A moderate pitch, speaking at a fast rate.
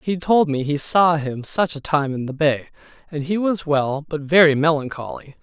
Yes: medium, 155 Hz; fast, 210 wpm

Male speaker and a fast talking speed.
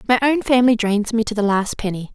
No: female; fast, 250 wpm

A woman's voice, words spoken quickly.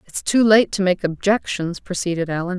No: female; average, 185 wpm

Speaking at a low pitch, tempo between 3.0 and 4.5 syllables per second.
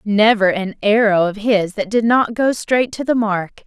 No: high, 215 Hz; 4.3 syllables/s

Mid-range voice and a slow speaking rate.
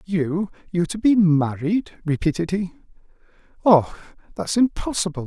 Yes: medium, 180 Hz; slow, 115 wpm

